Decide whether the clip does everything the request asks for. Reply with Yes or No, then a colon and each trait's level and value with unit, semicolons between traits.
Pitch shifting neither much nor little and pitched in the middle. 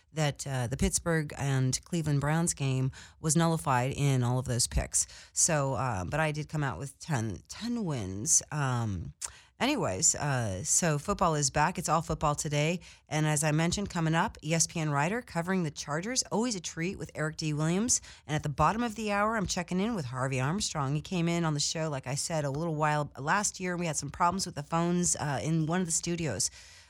Yes: average, 4.0 semitones; medium, 155 Hz